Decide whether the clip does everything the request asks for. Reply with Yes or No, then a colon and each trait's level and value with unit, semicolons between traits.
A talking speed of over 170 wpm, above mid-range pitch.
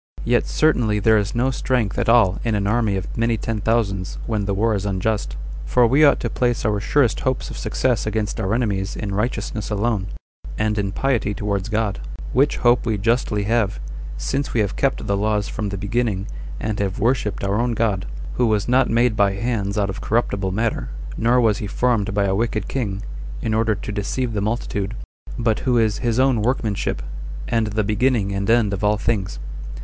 No: average, 200 wpm; low, 110 Hz